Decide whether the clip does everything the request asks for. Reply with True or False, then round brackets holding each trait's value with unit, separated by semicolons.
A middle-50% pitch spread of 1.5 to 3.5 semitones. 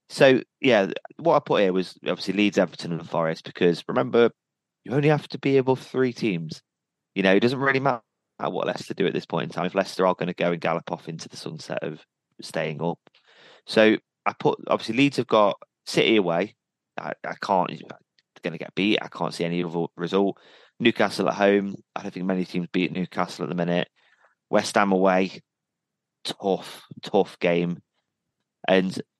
False (4.0 semitones)